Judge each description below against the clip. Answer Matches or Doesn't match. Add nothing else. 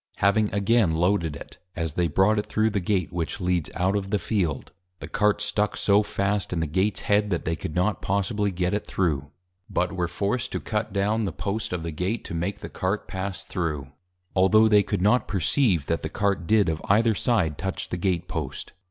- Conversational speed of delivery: Doesn't match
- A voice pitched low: Matches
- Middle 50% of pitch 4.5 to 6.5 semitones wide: Doesn't match